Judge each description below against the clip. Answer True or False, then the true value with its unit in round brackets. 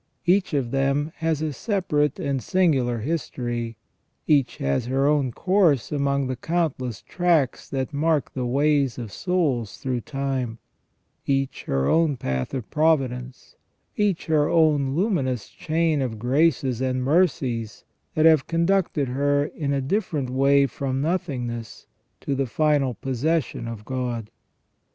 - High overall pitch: False (140 Hz)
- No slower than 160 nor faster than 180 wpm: False (135 wpm)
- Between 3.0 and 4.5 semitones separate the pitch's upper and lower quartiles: True (4.0 semitones)